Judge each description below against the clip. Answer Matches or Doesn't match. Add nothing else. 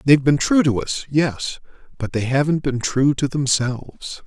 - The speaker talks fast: Doesn't match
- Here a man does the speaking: Matches